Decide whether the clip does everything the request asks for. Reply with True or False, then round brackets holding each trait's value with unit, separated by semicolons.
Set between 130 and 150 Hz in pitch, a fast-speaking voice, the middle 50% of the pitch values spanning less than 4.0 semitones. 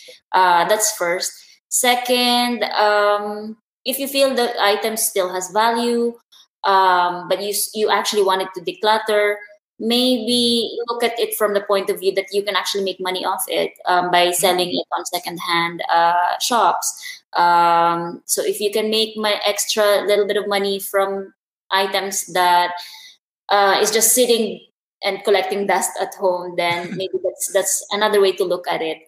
False (200 Hz; 165 wpm; 3.0 semitones)